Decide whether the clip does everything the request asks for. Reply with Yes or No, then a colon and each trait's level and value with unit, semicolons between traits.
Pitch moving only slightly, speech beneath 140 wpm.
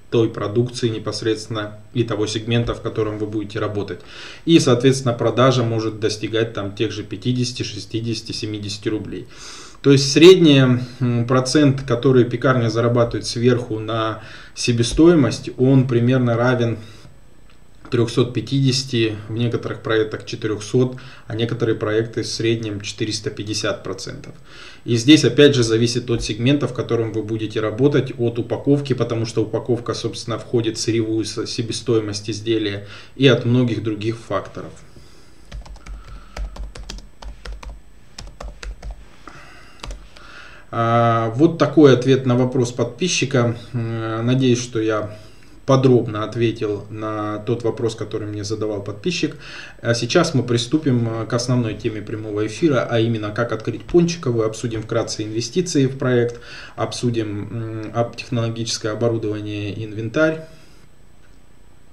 Yes: narrow, 2.3 semitones; average, 115 wpm